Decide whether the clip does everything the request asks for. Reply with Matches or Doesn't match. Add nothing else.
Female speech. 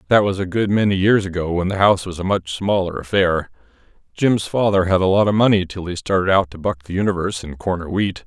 Doesn't match